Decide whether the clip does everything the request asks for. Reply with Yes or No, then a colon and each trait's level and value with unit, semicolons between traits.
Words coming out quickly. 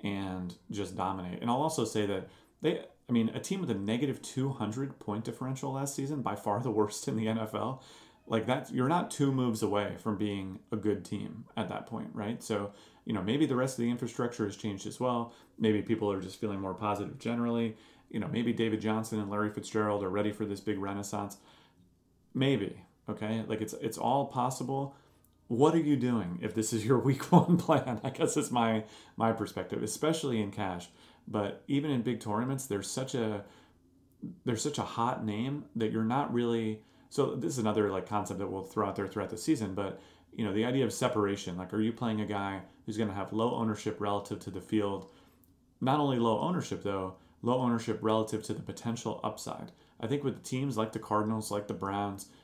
Yes: fast, 210 wpm